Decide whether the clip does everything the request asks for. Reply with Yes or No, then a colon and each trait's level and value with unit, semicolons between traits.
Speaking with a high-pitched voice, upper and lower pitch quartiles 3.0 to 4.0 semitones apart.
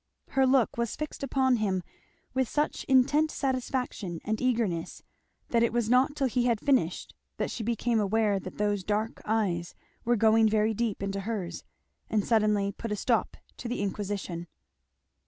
Yes: high, 225 Hz; average, 3.6 semitones